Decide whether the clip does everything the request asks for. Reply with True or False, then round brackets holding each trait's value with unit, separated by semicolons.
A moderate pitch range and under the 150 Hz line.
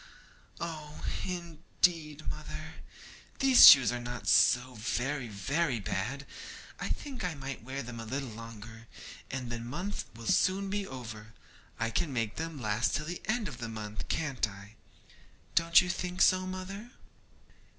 False (6.8 semitones; 135 Hz)